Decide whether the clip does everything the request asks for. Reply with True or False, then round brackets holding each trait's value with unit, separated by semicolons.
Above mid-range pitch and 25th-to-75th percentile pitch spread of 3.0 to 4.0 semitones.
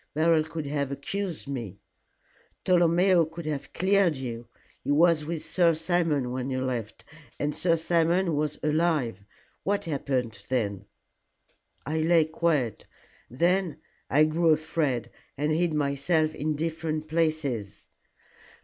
False (155 Hz; 3.4 semitones)